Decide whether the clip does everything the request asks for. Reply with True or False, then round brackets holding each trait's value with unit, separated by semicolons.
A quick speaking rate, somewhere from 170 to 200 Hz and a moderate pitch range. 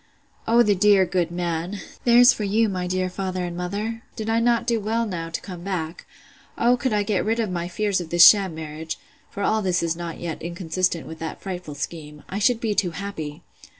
True (210 wpm; 185 Hz; 3.8 semitones)